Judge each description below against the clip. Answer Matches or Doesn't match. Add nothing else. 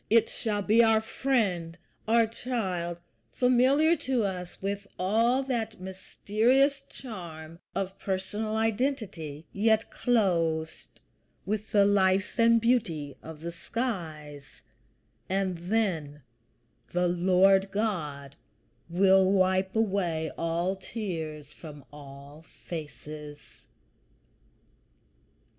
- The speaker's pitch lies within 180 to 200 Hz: Matches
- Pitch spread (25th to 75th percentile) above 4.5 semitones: Matches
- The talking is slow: Matches